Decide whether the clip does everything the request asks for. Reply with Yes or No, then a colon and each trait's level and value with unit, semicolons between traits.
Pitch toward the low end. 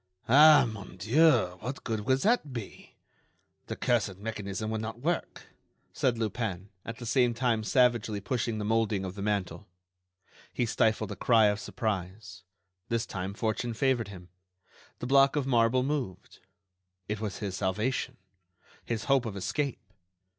Yes: low, 110 Hz